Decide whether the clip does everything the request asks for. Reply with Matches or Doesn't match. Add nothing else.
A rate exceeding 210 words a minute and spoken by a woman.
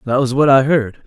Doesn't match